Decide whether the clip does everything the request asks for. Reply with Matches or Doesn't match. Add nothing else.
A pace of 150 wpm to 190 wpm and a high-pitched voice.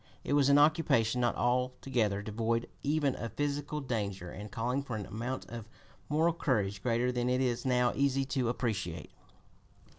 Doesn't match